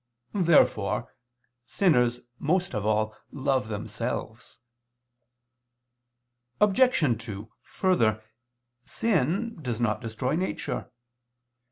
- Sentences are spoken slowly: Yes, slow, 75 wpm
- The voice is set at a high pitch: No, low, 125 Hz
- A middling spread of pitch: No, wide, 8.3 semitones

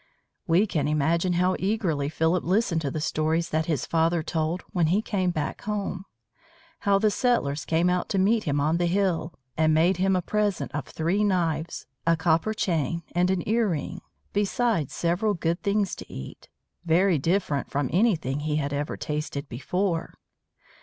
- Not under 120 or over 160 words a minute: No, average, 175 wpm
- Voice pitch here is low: No, medium, 170 Hz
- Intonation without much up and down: No, average, 3.7 semitones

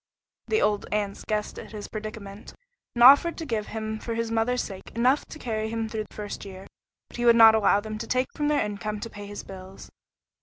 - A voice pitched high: Yes, high, 220 Hz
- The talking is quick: Yes, fast, 225 wpm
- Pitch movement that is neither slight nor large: No, narrow, 2.1 semitones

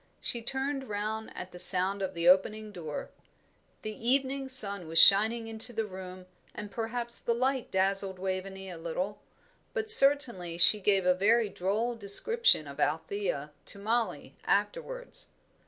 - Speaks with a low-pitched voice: No, high, 205 Hz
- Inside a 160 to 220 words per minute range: No, average, 150 wpm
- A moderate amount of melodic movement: Yes, average, 4.2 semitones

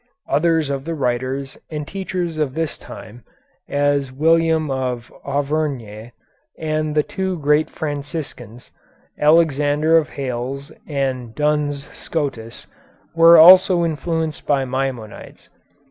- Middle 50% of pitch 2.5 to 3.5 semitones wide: Yes, average, 3.1 semitones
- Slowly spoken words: Yes, slow, 110 wpm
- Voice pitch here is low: No, medium, 145 Hz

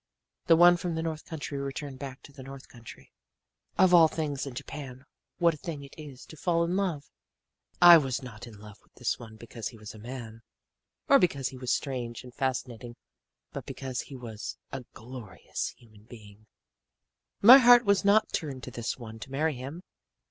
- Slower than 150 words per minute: No, average, 190 wpm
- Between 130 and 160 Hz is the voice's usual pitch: Yes, low, 135 Hz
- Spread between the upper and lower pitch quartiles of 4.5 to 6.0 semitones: Yes, average, 5.3 semitones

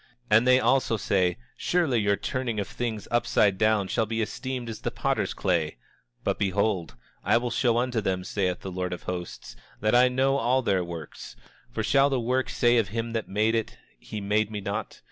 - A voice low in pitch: Yes, low, 110 Hz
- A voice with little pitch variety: No, average, 3.7 semitones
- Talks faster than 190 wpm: Yes, average, 200 wpm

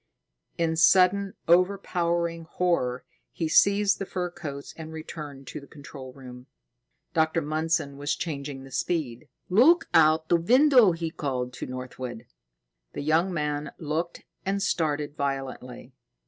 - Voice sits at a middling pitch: Yes, medium, 160 Hz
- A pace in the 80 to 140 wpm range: Yes, slow, 135 wpm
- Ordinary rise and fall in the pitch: Yes, average, 3.8 semitones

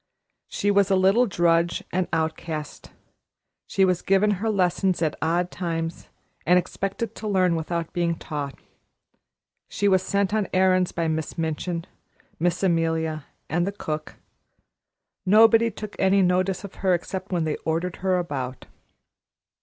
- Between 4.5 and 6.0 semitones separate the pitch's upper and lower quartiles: No, average, 2.8 semitones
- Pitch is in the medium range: Yes, medium, 180 Hz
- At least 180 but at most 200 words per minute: No, average, 145 wpm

